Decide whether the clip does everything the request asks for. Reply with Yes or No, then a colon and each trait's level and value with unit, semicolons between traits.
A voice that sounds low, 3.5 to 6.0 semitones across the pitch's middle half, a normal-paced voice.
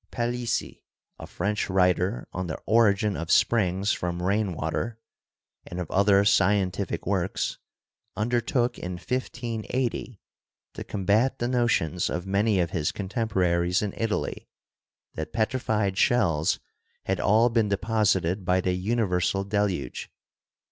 No: low, 100 Hz; average, 3.8 semitones; slow, 130 wpm